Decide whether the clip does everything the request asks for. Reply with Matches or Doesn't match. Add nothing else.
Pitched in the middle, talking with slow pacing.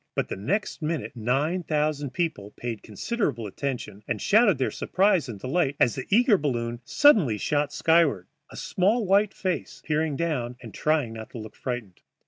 Doesn't match